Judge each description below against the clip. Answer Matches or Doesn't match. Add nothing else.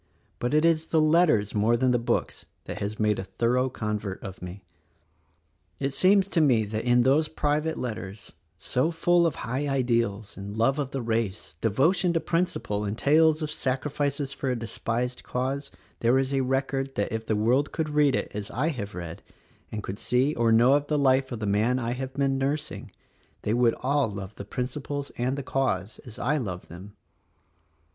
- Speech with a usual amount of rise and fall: Matches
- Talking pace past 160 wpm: Matches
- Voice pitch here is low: Matches